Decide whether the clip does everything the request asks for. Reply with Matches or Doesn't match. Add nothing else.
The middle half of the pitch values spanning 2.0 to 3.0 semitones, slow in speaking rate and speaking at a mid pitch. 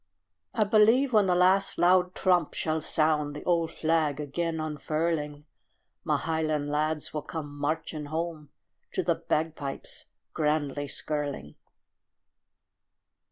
Matches